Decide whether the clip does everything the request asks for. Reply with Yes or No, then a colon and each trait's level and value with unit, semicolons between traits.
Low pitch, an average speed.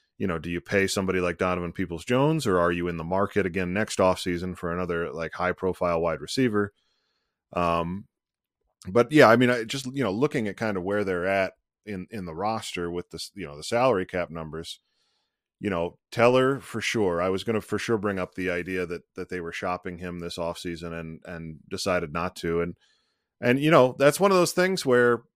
No: very low, 95 Hz; fast, 215 wpm